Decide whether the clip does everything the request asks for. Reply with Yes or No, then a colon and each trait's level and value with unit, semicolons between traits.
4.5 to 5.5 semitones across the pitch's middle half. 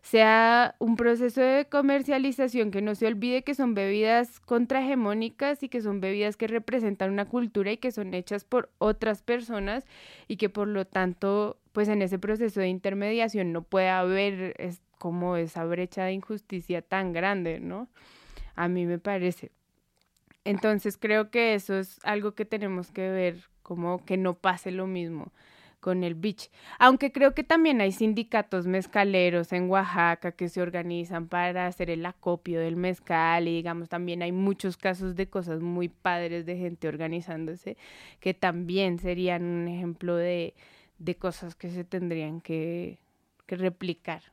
No: average, 3.5 semitones